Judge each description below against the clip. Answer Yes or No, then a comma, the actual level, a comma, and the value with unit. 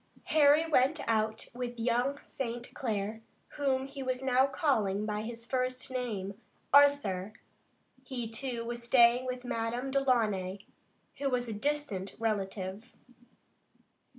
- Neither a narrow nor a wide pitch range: Yes, average, 3.5 semitones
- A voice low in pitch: No, high, 245 Hz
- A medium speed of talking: No, slow, 125 wpm